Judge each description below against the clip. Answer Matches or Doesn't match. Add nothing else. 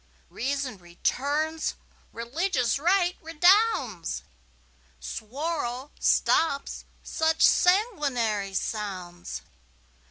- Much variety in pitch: Matches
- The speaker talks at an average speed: Doesn't match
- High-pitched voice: Matches